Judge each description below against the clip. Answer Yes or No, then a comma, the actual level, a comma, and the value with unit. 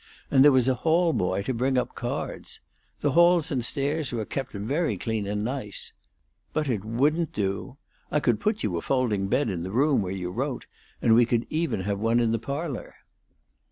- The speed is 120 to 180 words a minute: No, average, 200 wpm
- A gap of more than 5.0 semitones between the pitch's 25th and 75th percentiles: Yes, wide, 5.6 semitones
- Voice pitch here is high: No, low, 125 Hz